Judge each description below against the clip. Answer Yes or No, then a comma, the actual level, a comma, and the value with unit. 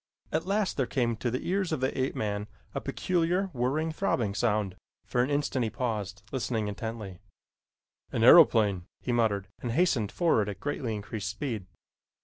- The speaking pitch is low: Yes, low, 120 Hz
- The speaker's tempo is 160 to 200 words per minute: Yes, average, 165 wpm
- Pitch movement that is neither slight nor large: No, wide, 5.7 semitones